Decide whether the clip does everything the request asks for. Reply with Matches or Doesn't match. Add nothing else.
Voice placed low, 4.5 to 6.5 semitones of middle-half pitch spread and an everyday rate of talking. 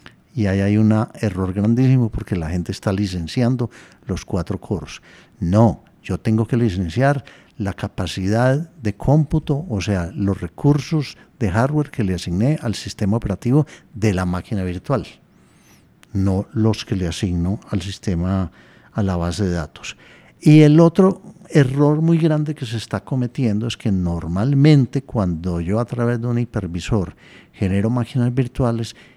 Matches